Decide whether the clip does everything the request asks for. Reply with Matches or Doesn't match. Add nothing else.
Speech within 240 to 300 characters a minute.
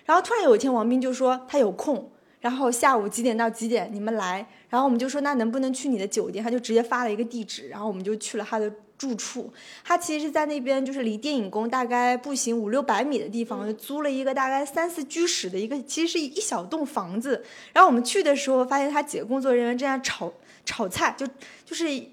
Doesn't match